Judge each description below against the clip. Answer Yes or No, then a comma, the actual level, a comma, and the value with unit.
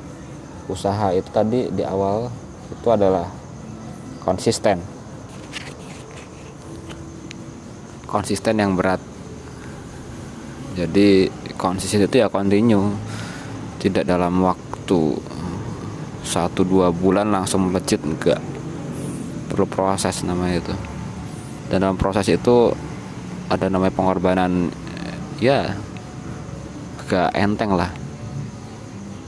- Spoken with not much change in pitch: Yes, narrow, 1.9 semitones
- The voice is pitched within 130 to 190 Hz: No, very low, 95 Hz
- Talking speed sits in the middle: No, slow, 80 wpm